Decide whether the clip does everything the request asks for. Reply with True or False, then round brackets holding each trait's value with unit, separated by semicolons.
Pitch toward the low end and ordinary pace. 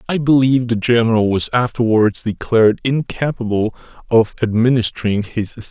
False (115 Hz; 125 wpm)